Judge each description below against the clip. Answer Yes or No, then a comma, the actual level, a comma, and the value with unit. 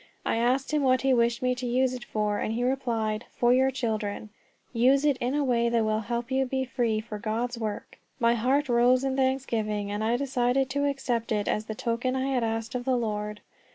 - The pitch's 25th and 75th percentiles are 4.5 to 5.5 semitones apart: No, average, 2.8 semitones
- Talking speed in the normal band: No, fast, 225 wpm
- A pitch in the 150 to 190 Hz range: No, high, 240 Hz